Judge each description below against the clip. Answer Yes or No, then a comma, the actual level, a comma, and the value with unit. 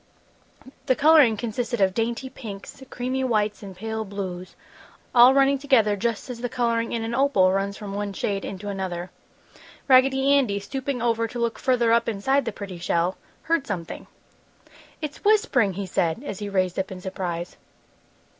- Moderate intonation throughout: Yes, average, 4.6 semitones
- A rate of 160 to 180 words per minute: Yes, average, 165 wpm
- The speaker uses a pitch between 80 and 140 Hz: No, high, 225 Hz